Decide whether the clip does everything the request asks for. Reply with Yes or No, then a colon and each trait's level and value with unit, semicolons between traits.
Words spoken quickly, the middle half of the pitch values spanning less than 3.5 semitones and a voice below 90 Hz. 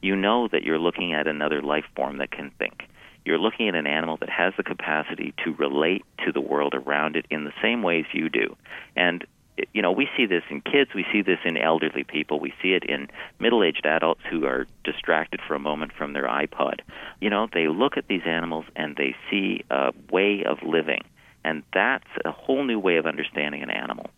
Yes: fast, 220 wpm; average, 2.8 semitones; very low, 80 Hz